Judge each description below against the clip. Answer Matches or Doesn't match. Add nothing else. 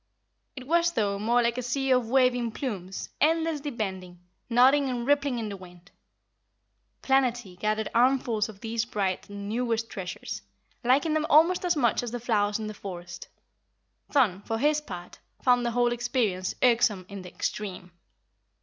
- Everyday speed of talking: Matches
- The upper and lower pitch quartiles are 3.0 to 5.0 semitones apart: Matches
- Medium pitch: Doesn't match